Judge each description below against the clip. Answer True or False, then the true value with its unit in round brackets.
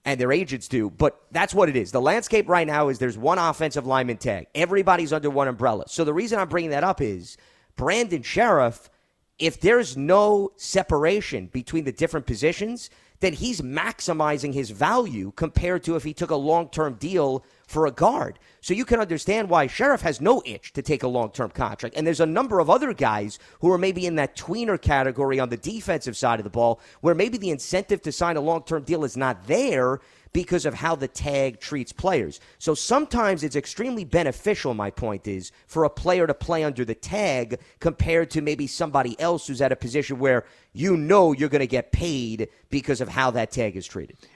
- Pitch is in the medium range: True (150 Hz)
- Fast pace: True (210 wpm)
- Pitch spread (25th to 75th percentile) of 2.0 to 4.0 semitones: False (5.1 semitones)